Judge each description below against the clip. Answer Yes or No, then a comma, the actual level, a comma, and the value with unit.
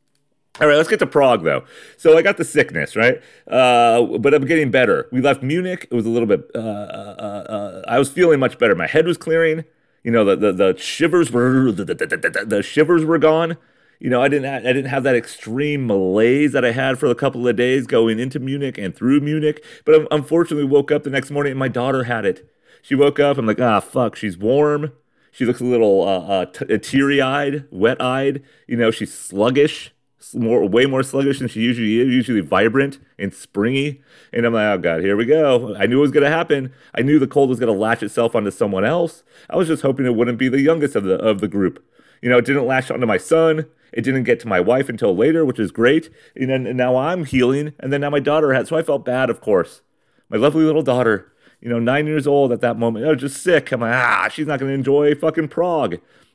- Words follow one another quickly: Yes, fast, 240 wpm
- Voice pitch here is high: No, low, 135 Hz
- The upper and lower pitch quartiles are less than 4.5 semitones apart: Yes, average, 3.5 semitones